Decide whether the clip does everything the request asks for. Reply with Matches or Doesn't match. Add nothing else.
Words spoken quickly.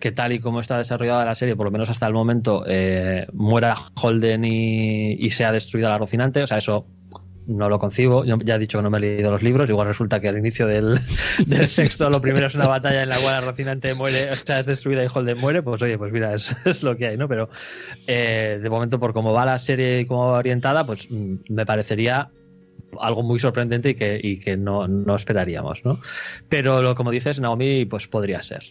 Matches